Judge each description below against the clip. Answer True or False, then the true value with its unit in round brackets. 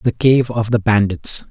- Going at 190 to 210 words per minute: True (200 wpm)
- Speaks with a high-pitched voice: False (110 Hz)